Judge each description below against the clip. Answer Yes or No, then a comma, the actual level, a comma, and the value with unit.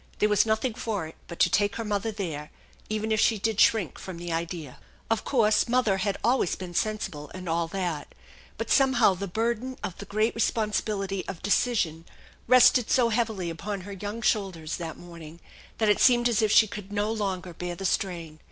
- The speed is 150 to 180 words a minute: No, average, 195 wpm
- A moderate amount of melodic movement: Yes, average, 4.1 semitones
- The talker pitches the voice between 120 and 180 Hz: No, high, 205 Hz